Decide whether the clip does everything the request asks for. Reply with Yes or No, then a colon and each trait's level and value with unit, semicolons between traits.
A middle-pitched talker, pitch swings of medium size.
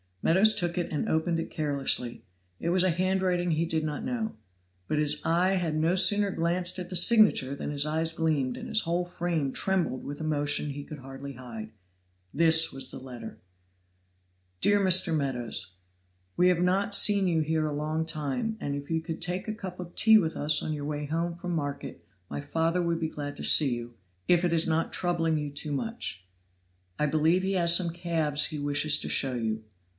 Yes: medium, 160 Hz; average, 3.5 semitones